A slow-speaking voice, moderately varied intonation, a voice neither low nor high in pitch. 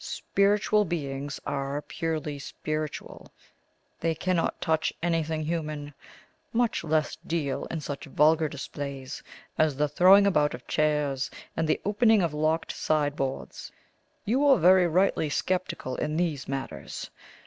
Yes: slow, 125 wpm; average, 3.3 semitones; medium, 155 Hz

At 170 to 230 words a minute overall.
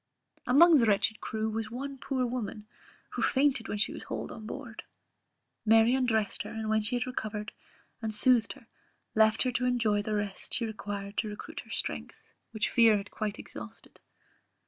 Yes: average, 180 wpm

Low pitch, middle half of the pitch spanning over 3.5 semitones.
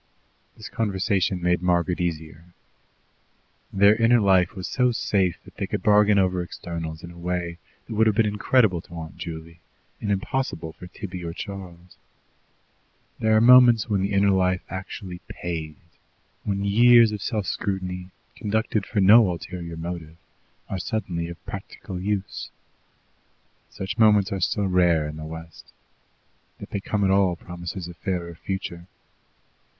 No: very low, 95 Hz; average, 3.1 semitones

